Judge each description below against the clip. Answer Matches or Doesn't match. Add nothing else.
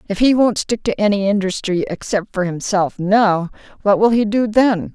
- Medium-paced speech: Matches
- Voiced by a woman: Matches